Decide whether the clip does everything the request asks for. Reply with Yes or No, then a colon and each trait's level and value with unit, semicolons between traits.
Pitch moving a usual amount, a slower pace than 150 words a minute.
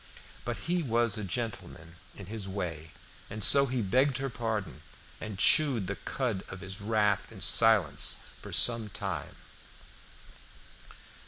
Yes: average, 3.9 semitones; average, 140 wpm